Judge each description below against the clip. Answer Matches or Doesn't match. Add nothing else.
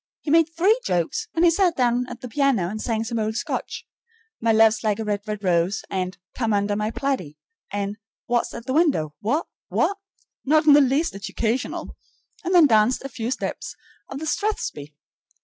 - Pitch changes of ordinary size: Doesn't match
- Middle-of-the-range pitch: Doesn't match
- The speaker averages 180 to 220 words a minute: Matches